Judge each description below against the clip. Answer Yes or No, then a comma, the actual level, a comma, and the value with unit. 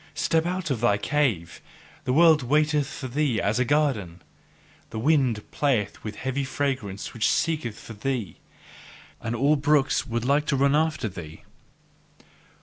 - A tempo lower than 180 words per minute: Yes, average, 150 wpm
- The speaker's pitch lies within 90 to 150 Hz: Yes, low, 135 Hz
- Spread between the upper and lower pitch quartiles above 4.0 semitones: Yes, average, 5.0 semitones